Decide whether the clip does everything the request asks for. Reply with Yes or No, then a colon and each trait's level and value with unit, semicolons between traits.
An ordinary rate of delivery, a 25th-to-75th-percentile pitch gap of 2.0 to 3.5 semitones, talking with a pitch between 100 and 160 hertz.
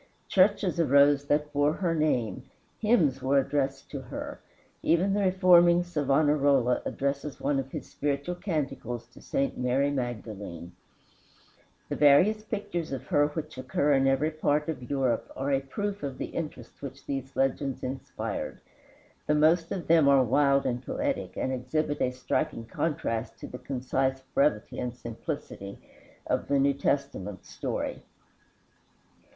Yes: average, 145 wpm; average, 3.1 semitones; medium, 140 Hz